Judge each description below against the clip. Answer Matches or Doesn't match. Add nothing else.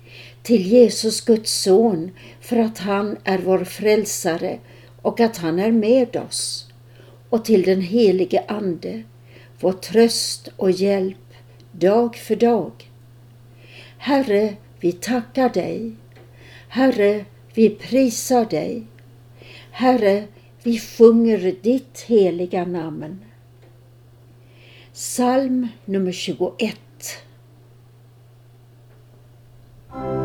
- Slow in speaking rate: Matches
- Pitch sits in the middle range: Matches